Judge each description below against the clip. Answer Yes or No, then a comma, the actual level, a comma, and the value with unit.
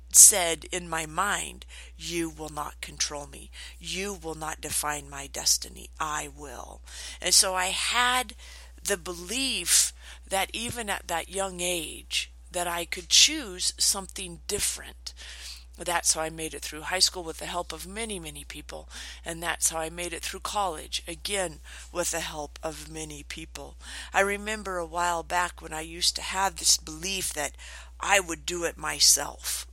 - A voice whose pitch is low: No, medium, 160 Hz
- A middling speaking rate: Yes, average, 170 wpm